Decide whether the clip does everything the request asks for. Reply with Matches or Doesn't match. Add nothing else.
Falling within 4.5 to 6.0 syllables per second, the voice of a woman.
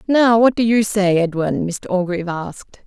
Matches